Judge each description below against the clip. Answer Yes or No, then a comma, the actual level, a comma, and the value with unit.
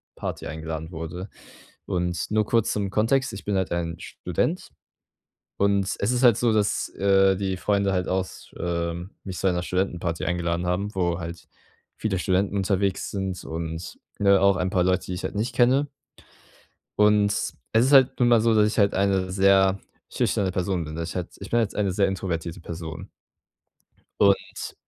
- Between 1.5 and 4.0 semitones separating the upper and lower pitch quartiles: Yes, narrow, 2.6 semitones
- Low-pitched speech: Yes, very low, 95 Hz